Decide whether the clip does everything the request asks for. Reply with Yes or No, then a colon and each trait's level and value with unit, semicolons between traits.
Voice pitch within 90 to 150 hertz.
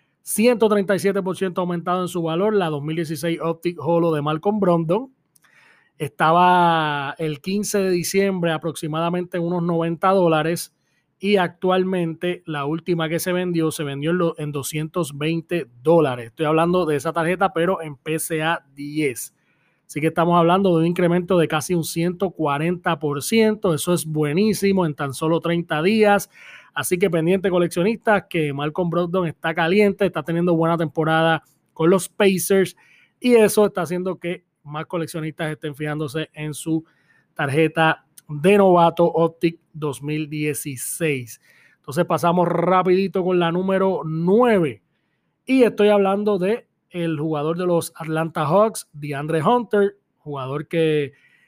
No: medium, 170 Hz